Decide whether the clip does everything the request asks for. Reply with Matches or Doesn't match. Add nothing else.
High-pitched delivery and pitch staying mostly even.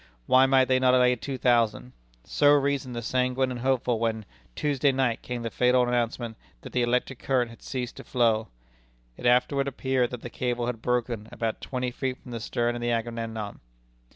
Doesn't match